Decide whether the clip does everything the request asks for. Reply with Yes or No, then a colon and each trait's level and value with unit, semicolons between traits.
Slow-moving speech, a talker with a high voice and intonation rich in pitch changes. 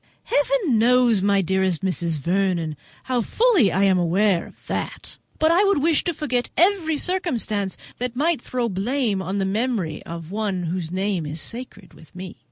No: average, 175 wpm; high, 205 Hz; wide, 6.0 semitones